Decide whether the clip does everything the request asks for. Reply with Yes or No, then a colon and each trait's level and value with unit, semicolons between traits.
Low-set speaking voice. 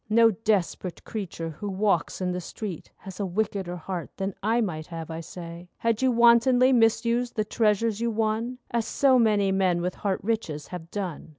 No: high, 205 Hz